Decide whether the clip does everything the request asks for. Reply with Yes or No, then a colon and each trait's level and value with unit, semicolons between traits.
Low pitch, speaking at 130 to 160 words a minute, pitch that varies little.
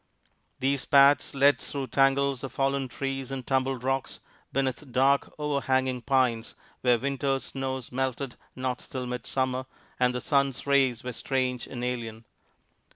Yes: low, 130 Hz; average, 140 wpm; narrow, 1.5 semitones